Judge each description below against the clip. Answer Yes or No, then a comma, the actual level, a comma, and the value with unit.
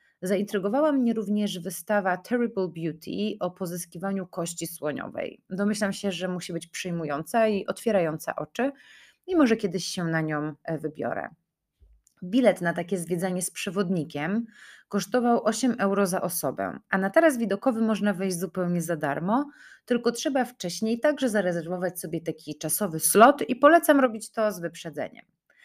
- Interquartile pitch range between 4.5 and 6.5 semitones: Yes, average, 4.8 semitones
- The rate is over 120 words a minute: Yes, average, 145 wpm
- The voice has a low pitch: No, high, 195 Hz